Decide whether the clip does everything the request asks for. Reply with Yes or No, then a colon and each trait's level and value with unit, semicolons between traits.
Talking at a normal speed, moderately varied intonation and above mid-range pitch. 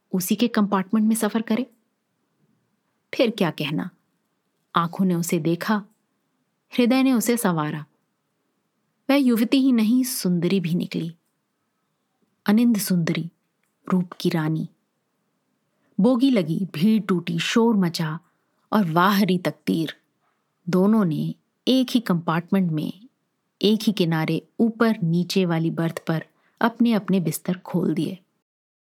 Yes: average, 120 wpm; average, 4.8 semitones; high, 195 Hz